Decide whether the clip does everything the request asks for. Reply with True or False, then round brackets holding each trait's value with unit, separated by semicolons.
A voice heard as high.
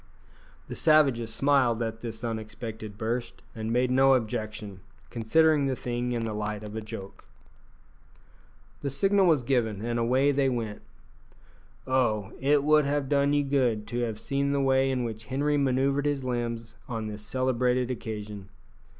False (125 Hz)